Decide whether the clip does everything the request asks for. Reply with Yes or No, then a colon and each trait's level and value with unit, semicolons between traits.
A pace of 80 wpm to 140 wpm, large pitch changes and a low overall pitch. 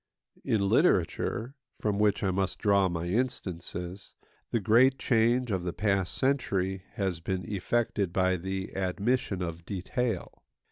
No: slow, 135 wpm; average, 3.4 semitones; very low, 95 Hz